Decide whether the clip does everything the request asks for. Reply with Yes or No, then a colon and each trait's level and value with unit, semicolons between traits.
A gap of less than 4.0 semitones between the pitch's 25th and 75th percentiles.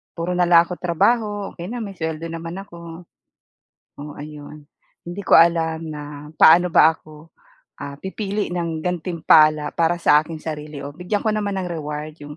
Yes: narrow, 2.6 semitones